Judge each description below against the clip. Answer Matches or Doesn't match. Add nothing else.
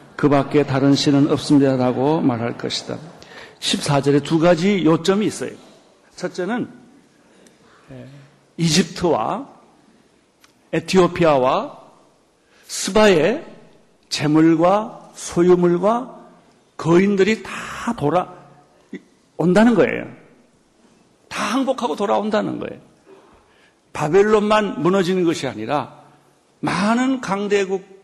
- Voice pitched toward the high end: Doesn't match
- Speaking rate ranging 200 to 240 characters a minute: Matches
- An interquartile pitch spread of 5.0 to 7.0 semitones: Matches